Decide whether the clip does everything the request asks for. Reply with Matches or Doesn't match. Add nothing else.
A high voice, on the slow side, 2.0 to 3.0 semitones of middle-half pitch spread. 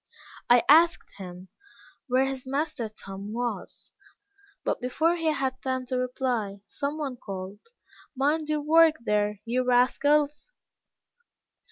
Doesn't match